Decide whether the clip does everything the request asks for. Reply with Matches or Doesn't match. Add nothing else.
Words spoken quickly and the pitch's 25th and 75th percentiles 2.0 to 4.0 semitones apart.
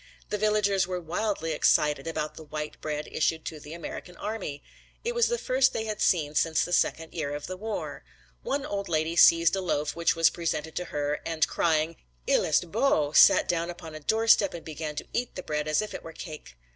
Doesn't match